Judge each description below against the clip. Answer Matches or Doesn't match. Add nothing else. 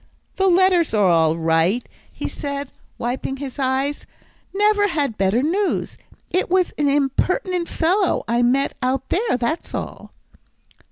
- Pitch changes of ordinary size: Doesn't match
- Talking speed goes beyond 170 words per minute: Doesn't match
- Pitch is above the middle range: Matches